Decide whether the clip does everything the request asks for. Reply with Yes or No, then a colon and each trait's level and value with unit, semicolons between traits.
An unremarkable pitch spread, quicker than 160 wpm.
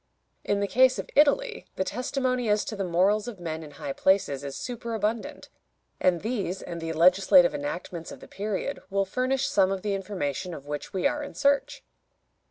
No: wide, 5.7 semitones; average, 185 wpm